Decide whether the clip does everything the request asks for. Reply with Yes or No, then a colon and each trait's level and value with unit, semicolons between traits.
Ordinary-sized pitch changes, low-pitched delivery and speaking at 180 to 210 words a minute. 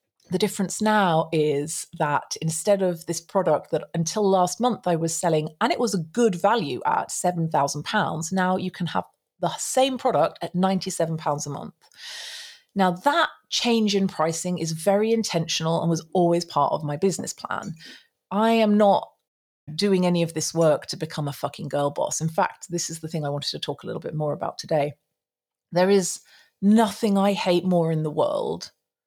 No: average, 4.0 semitones; medium, 175 Hz; average, 185 wpm